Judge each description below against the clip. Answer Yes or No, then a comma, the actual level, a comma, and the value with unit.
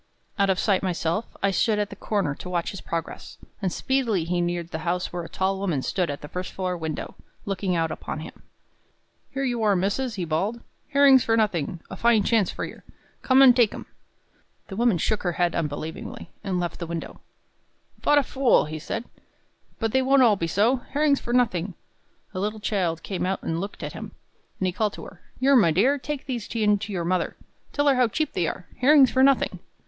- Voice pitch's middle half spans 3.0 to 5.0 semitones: No, wide, 5.6 semitones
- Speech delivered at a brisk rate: Yes, fast, 215 wpm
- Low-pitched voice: No, high, 200 Hz